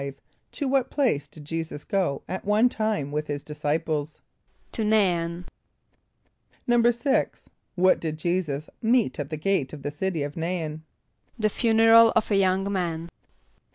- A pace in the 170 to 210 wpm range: No, average, 150 wpm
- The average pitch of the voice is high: No, medium, 180 Hz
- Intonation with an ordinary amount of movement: No, wide, 6.1 semitones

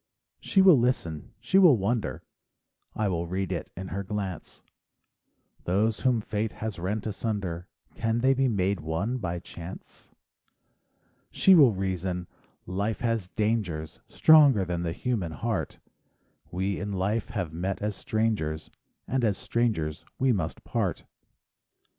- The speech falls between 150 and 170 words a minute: No, slow, 135 wpm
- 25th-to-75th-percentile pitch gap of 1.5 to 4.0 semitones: No, average, 4.4 semitones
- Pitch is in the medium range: No, low, 100 Hz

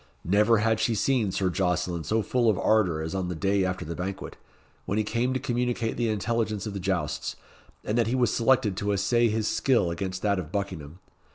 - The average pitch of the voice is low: Yes, low, 105 Hz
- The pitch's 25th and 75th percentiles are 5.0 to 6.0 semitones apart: No, average, 3.8 semitones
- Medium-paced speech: No, fast, 210 wpm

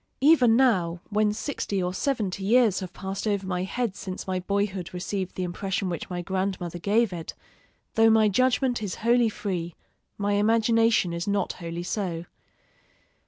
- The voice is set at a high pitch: Yes, high, 200 Hz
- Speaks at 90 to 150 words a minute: No, average, 160 wpm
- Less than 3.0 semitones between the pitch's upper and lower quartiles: No, average, 3.7 semitones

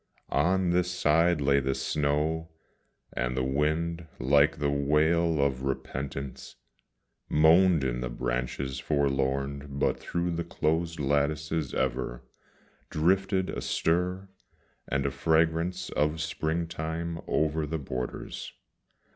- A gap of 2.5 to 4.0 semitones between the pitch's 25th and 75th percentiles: Yes, average, 3.3 semitones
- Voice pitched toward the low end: Yes, very low, 75 Hz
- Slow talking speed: Yes, slow, 115 wpm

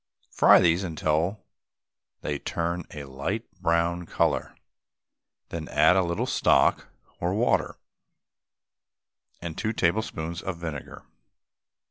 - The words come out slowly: Yes, slow, 105 wpm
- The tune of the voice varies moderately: No, narrow, 2.2 semitones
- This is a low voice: Yes, very low, 85 Hz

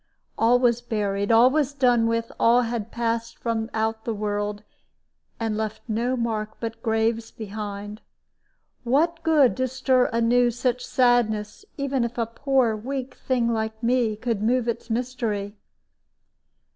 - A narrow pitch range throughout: Yes, narrow, 2.2 semitones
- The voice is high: Yes, high, 230 Hz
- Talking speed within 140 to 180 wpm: Yes, average, 145 wpm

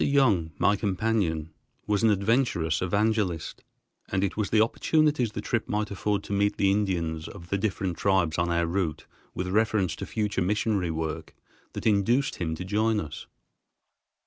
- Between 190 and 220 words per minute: No, average, 165 wpm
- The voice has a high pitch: No, low, 100 Hz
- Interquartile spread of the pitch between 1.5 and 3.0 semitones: No, average, 3.9 semitones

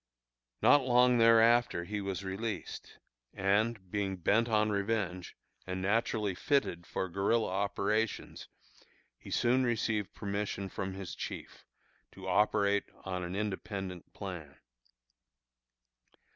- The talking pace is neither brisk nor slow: No, slow, 110 wpm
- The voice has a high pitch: No, low, 100 Hz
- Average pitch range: Yes, average, 3.0 semitones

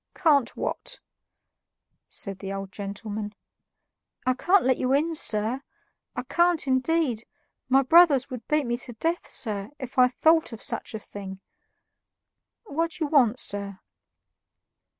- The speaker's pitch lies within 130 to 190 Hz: No, very high, 255 Hz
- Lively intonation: Yes, wide, 6.3 semitones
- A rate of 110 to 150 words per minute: Yes, average, 140 wpm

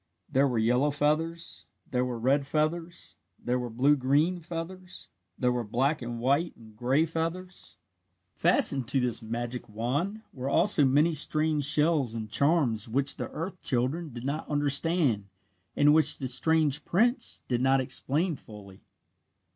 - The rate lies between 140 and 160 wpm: Yes, average, 150 wpm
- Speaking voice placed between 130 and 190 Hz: Yes, medium, 140 Hz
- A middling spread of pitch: Yes, average, 4.7 semitones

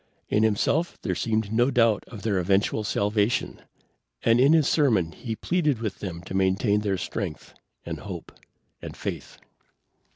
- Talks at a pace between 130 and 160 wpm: Yes, average, 155 wpm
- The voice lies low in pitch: Yes, low, 110 Hz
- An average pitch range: Yes, average, 3.5 semitones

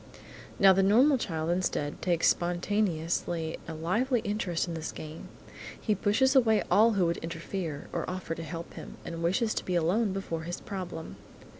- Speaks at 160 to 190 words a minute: Yes, average, 170 wpm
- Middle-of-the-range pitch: Yes, medium, 180 Hz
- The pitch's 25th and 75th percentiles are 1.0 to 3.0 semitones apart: No, average, 3.8 semitones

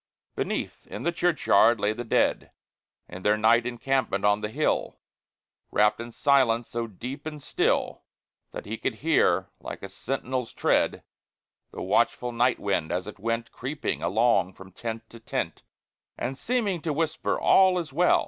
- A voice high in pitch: No, low, 120 Hz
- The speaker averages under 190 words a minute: Yes, average, 160 wpm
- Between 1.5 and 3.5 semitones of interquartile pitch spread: No, average, 4.7 semitones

